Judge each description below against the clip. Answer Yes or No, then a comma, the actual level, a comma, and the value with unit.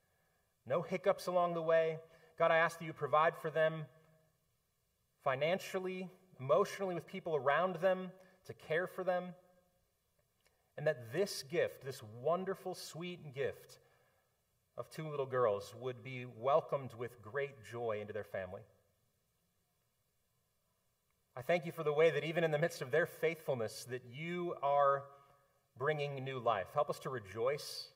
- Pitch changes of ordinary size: Yes, average, 4.3 semitones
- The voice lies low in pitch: No, medium, 160 Hz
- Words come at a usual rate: Yes, average, 145 wpm